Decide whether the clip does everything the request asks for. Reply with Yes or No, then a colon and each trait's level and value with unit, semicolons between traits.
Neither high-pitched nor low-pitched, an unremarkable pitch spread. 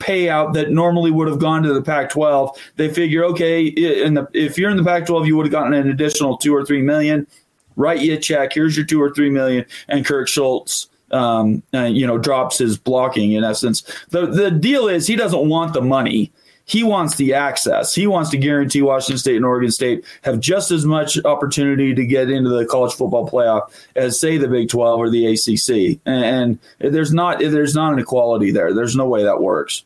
Yes: medium, 145 Hz; average, 3.6 semitones